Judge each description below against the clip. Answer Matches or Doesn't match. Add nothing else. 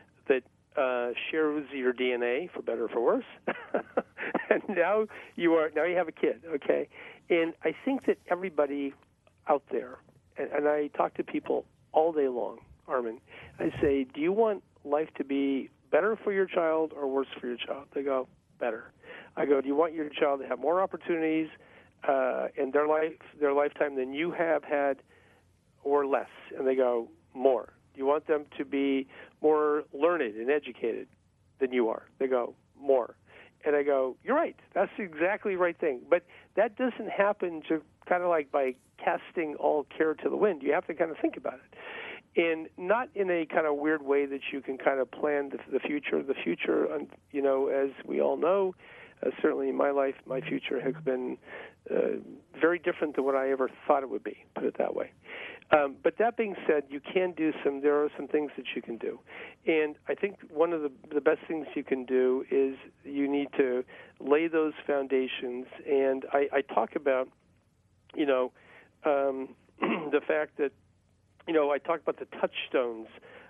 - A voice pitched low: Doesn't match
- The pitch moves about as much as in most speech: Matches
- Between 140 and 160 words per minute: Doesn't match